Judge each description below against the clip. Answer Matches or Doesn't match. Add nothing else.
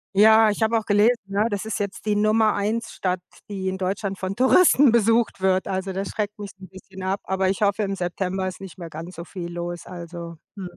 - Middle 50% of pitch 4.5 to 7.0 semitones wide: Doesn't match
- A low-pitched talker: Doesn't match